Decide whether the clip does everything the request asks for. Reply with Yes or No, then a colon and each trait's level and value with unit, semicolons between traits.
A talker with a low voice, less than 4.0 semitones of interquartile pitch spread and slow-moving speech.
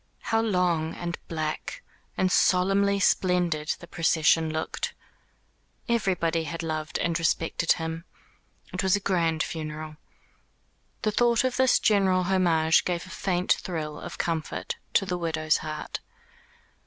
No: medium, 170 Hz; average, 2.8 semitones; slow, 130 wpm